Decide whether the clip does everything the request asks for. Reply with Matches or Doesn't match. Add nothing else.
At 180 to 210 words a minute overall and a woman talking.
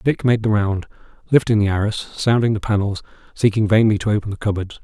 Doesn't match